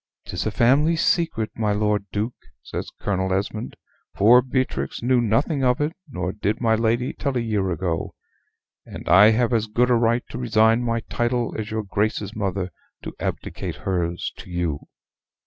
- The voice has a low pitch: Yes, low, 110 Hz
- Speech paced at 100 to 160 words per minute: No, average, 170 wpm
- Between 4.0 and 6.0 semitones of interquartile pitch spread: No, average, 3.3 semitones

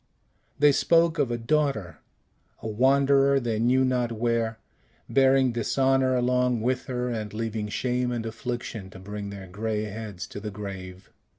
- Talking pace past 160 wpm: No, average, 155 wpm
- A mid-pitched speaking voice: No, low, 120 Hz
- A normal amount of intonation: Yes, average, 3.5 semitones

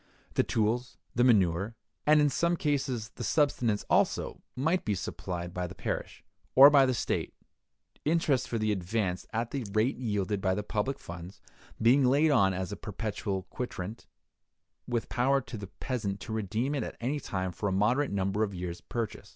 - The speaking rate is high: No, average, 180 wpm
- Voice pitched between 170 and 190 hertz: No, low, 110 Hz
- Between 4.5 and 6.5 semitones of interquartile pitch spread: Yes, average, 5.1 semitones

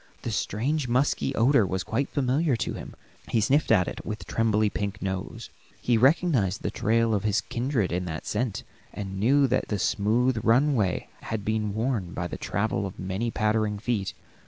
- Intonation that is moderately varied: Yes, average, 3.8 semitones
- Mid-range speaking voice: No, low, 110 Hz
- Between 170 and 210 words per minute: Yes, average, 180 wpm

